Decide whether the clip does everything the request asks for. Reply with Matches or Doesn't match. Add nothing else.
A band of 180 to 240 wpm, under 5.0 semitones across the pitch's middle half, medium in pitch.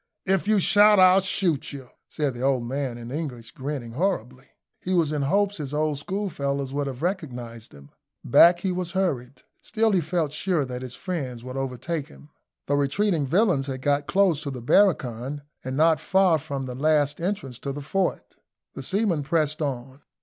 Doesn't match